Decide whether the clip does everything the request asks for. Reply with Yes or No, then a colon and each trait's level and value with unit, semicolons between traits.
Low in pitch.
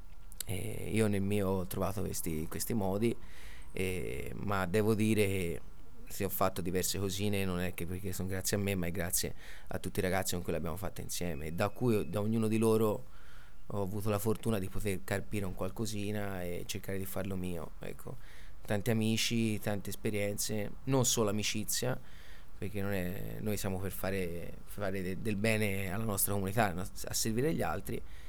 Yes: low, 100 Hz